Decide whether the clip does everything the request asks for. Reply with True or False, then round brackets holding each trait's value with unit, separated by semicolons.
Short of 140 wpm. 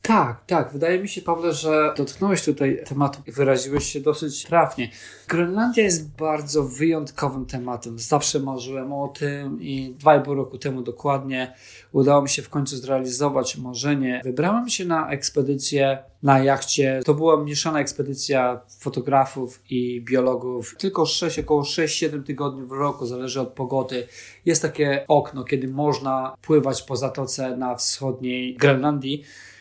False (145 wpm)